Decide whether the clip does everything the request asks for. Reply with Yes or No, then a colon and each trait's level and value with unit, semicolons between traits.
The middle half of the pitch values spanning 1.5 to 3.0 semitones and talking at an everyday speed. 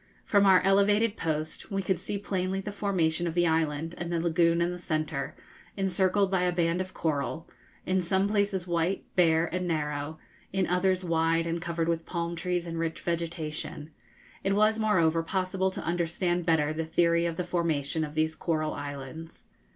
Yes: narrow, 2.5 semitones; average, 180 wpm